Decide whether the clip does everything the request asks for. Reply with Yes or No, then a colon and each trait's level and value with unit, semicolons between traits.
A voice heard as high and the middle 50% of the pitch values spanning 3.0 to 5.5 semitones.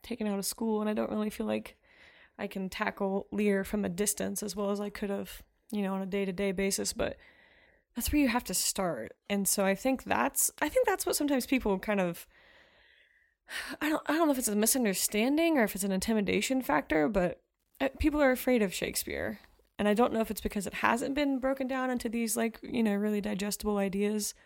Yes: high, 215 Hz; average, 4.3 semitones